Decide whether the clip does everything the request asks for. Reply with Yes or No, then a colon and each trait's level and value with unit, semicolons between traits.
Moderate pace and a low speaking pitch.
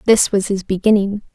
No: average, 180 wpm; high, 200 Hz